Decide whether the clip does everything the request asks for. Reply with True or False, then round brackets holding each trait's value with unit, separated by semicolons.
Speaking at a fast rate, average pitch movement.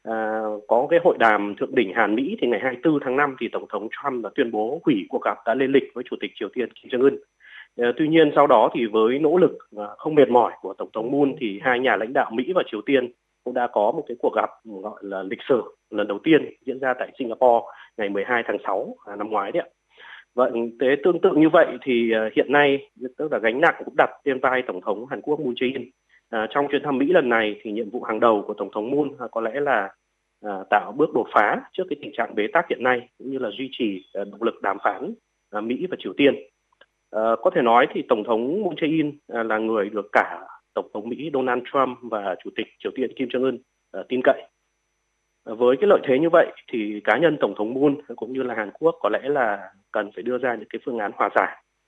True (255 wpm; 4.2 semitones)